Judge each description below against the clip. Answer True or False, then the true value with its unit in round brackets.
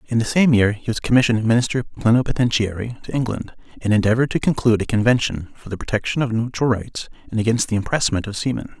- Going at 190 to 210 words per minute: True (200 wpm)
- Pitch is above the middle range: False (115 Hz)